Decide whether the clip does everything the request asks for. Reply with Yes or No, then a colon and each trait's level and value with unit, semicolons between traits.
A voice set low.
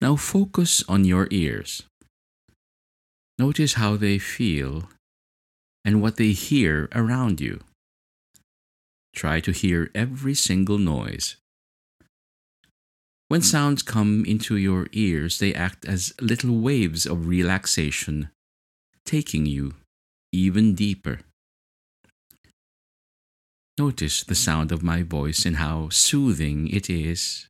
Yes: very low, 90 Hz